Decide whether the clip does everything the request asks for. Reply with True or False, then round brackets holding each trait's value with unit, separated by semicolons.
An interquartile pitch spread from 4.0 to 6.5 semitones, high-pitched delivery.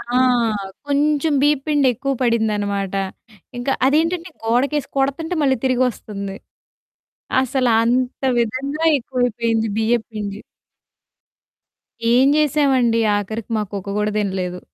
True (4.3 semitones; 245 Hz)